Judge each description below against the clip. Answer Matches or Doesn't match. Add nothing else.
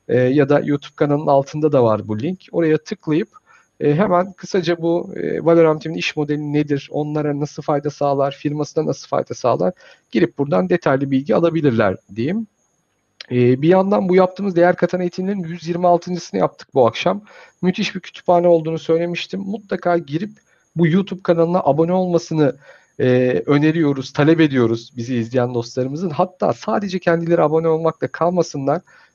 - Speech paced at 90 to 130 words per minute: Doesn't match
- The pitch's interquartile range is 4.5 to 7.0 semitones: Doesn't match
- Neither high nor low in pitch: Matches